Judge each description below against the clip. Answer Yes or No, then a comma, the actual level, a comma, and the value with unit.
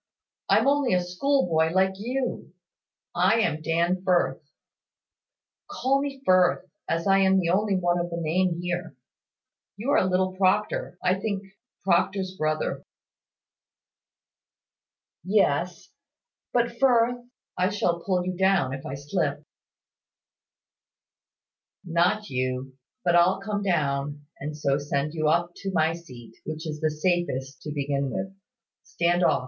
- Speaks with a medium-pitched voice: Yes, medium, 175 Hz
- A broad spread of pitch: No, average, 3.8 semitones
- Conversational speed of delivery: No, slow, 130 wpm